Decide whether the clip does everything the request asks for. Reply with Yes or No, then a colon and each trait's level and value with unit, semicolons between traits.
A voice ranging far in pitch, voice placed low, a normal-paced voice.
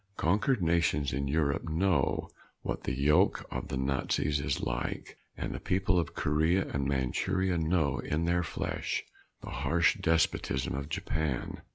No: average, 3.7 semitones; very low, 80 Hz; average, 155 wpm